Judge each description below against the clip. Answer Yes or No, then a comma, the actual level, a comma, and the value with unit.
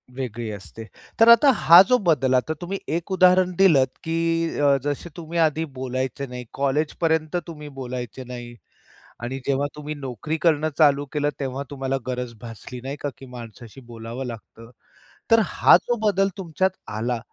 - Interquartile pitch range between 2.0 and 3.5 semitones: No, average, 4.7 semitones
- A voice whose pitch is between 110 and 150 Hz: Yes, medium, 140 Hz